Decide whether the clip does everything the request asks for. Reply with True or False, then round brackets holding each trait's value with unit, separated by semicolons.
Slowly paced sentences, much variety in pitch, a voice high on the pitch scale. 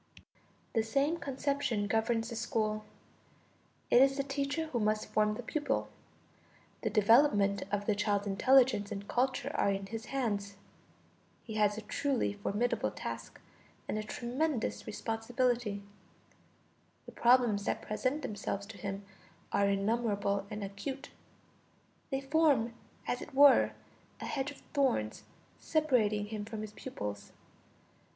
False (130 wpm; 4.5 semitones; 225 Hz)